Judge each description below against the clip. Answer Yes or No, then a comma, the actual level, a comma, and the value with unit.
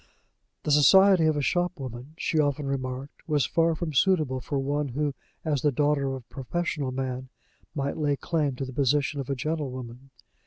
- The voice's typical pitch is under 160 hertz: Yes, medium, 140 Hz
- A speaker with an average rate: Yes, average, 180 wpm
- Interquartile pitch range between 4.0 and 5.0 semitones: No, average, 2.7 semitones